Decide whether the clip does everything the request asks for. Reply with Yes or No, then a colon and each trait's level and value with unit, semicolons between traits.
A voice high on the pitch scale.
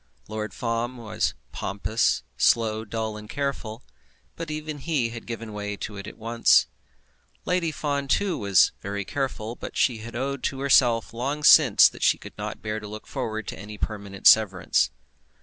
No: low, 115 Hz